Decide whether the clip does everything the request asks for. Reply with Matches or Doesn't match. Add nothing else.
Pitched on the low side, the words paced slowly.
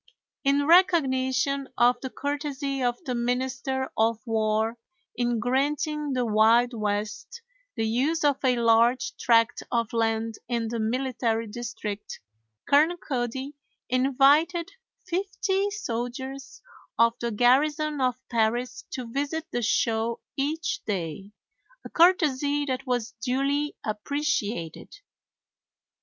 Doesn't match